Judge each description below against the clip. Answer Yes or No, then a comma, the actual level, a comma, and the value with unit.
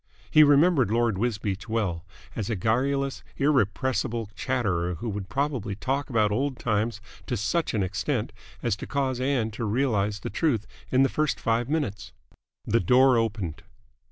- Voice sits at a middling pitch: No, low, 115 Hz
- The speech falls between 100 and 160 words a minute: Yes, average, 155 wpm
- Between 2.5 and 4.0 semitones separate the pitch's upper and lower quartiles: No, average, 4.4 semitones